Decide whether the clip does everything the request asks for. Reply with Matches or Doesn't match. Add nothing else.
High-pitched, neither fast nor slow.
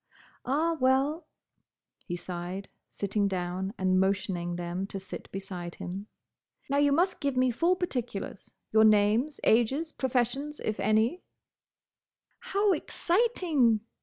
Doesn't match